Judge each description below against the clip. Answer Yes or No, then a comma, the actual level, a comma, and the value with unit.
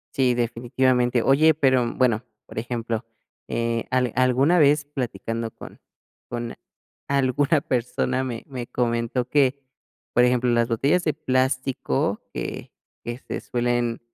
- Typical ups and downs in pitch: No, narrow, 2.2 semitones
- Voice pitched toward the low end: Yes, low, 125 Hz